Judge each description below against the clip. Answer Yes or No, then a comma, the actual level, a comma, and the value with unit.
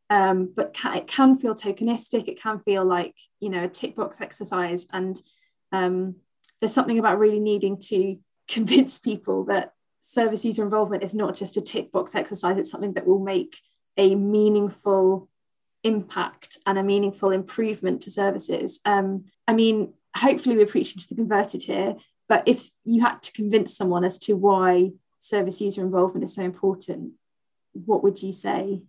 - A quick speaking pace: No, average, 170 wpm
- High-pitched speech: Yes, high, 200 Hz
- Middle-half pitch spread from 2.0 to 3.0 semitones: Yes, average, 2.7 semitones